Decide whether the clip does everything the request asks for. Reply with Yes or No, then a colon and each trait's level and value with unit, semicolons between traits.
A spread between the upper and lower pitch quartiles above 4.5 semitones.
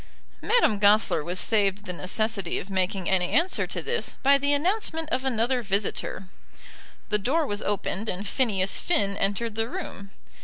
Yes: average, 5.2 semitones